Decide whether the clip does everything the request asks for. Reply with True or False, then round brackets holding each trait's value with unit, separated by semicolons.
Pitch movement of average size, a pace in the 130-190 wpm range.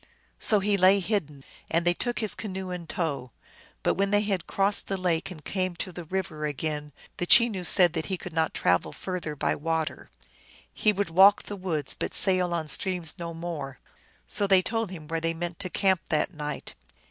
False (3.2 semitones; 200 wpm)